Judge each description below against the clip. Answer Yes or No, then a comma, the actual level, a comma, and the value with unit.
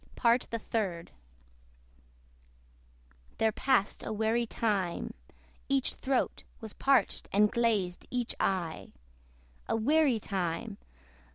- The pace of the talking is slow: Yes, slow, 100 wpm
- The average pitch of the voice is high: Yes, high, 220 Hz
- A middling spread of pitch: Yes, average, 3.3 semitones